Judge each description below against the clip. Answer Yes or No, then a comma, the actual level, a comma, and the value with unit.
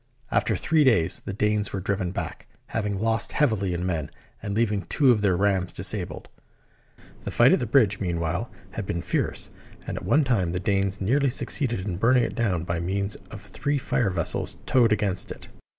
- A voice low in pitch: Yes, low, 100 Hz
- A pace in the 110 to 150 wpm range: No, average, 190 wpm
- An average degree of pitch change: Yes, average, 3.9 semitones